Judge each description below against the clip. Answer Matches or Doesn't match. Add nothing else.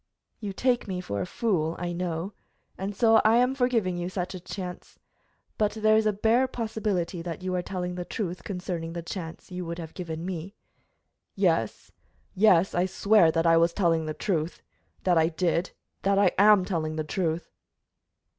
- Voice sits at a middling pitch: Matches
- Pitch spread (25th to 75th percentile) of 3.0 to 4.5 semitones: Matches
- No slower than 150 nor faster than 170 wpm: Doesn't match